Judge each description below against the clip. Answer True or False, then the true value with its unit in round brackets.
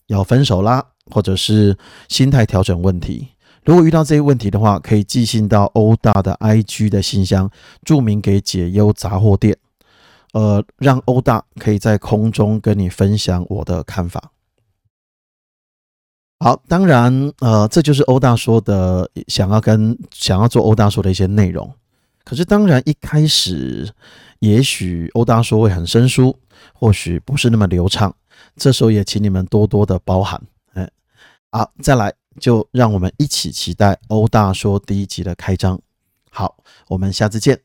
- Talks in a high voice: False (105 Hz)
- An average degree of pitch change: True (3.9 semitones)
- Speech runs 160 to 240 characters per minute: True (235 characters per minute)